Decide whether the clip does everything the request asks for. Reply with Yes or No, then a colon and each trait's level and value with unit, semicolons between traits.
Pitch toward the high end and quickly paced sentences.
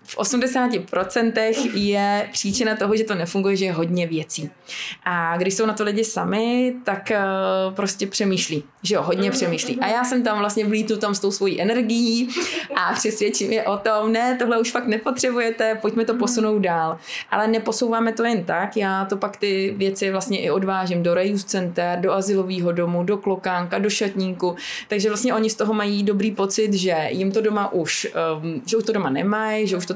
Yes: high, 205 Hz; fast, 190 wpm